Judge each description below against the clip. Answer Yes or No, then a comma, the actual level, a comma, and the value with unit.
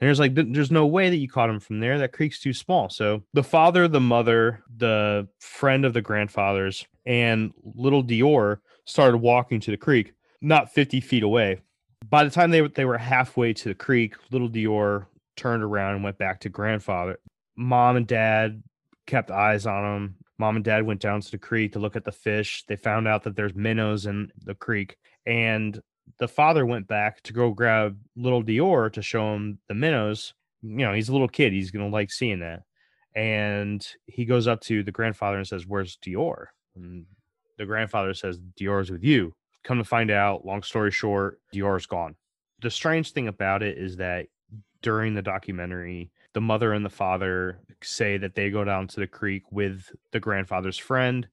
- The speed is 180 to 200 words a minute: Yes, average, 195 wpm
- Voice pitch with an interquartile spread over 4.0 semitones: No, average, 3.2 semitones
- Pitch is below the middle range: Yes, low, 110 Hz